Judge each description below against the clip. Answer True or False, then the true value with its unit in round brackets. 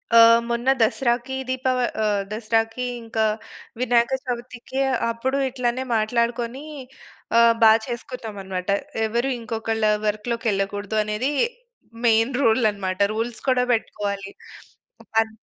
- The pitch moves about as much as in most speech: False (2.3 semitones)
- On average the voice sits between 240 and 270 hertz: False (230 Hz)